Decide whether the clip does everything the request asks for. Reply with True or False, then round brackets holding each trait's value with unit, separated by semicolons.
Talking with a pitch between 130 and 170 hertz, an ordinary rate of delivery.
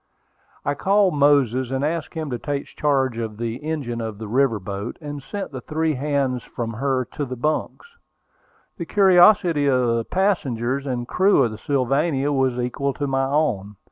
True (135 Hz; 175 wpm)